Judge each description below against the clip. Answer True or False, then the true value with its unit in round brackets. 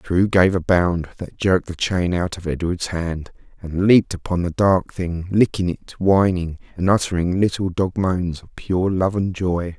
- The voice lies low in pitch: True (90 Hz)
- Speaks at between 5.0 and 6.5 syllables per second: False (4.4 syllables/s)